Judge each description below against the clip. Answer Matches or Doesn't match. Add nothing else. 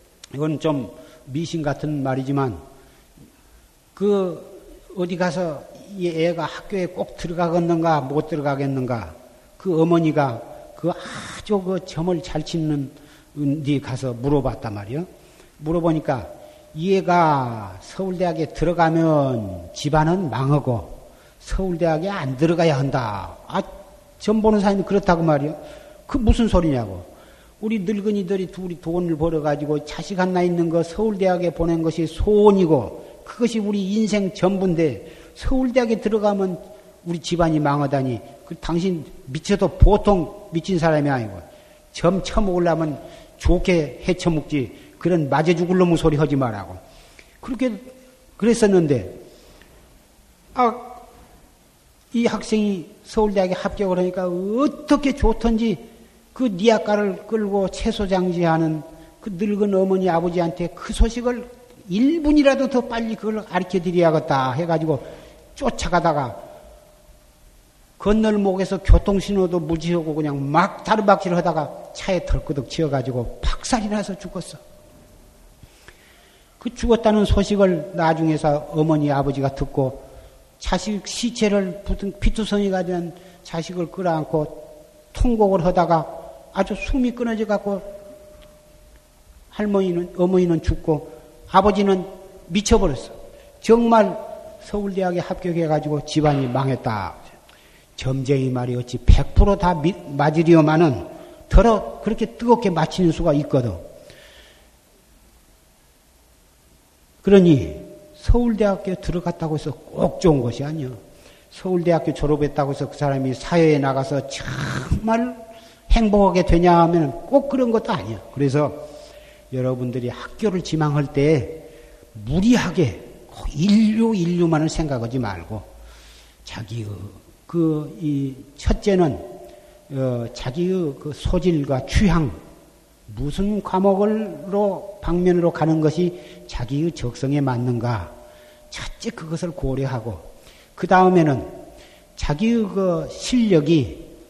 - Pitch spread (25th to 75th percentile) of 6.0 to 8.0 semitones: Doesn't match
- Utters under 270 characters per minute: Matches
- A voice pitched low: Doesn't match